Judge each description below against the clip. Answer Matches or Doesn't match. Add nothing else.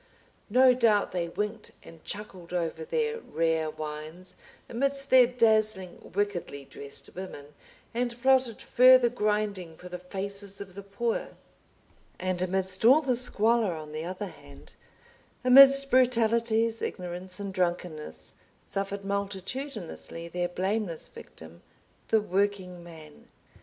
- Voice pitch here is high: Matches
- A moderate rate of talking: Doesn't match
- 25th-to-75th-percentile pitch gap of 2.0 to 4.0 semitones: Doesn't match